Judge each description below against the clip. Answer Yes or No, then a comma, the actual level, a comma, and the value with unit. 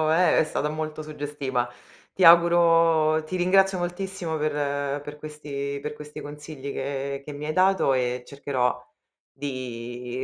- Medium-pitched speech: Yes, medium, 150 Hz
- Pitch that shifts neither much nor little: Yes, average, 3.1 semitones